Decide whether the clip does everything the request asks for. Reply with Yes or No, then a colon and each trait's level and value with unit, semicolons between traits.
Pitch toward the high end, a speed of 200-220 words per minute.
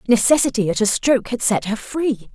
Yes: high, 235 Hz; fast, 205 wpm